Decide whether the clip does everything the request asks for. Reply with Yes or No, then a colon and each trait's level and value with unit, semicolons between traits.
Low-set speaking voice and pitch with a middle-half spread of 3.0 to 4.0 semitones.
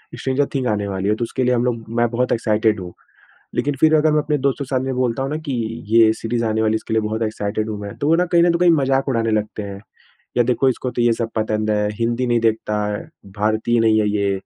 Yes: low, 115 Hz; average, 3.4 semitones